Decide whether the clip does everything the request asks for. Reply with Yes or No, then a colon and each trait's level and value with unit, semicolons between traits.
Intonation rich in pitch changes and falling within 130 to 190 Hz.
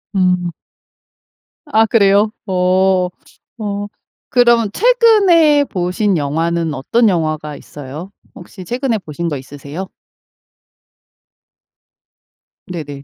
Yes: wide, 5.7 semitones; medium, 185 Hz